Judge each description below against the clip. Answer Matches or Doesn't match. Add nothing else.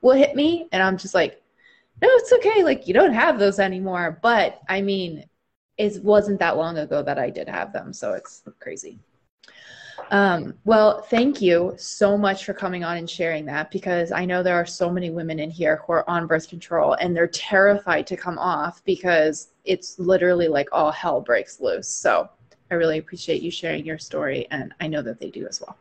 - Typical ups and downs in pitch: Matches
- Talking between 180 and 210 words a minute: Matches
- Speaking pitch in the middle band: Matches